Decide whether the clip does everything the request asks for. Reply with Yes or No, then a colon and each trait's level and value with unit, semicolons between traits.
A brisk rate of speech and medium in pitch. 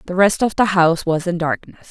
Yes: fast, 250 wpm; medium, 180 Hz